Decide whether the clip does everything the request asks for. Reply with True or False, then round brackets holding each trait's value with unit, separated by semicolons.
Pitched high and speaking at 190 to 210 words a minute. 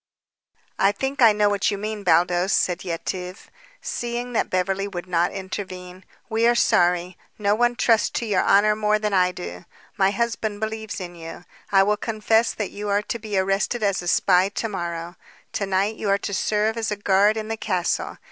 True (200 Hz; 195 wpm)